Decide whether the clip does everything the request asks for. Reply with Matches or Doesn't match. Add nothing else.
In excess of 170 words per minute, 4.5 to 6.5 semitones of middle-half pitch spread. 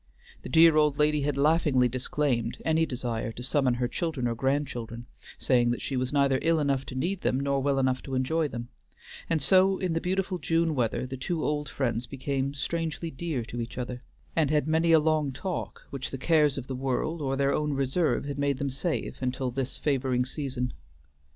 Doesn't match